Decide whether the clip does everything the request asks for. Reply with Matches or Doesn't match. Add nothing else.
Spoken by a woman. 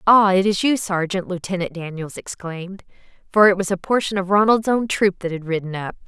Matches